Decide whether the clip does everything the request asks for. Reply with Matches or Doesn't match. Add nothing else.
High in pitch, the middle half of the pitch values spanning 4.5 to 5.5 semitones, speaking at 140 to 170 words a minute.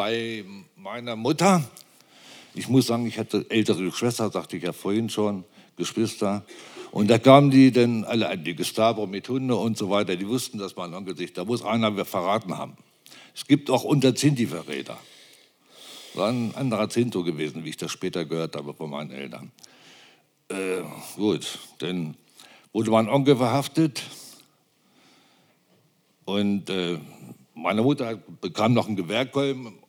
Doesn't match